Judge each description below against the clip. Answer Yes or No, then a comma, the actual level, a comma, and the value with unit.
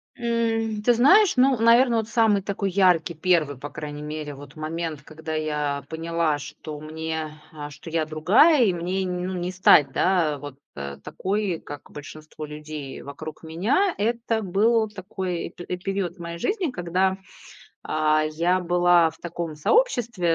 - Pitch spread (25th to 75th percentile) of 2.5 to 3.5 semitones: No, average, 5.0 semitones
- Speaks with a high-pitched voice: No, medium, 175 Hz